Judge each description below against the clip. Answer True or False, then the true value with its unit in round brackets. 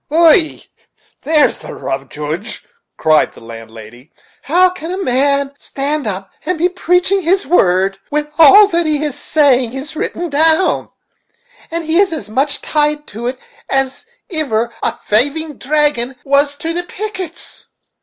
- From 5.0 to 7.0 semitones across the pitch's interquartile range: True (5.5 semitones)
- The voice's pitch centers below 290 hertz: False (295 Hz)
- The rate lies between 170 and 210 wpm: False (150 wpm)